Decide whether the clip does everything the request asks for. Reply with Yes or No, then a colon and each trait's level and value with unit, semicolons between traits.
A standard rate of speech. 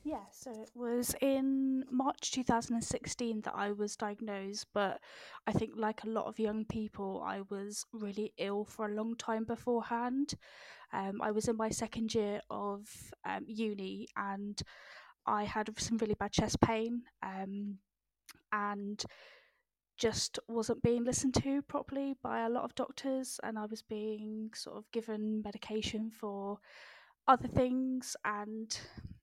Yes: average, 155 wpm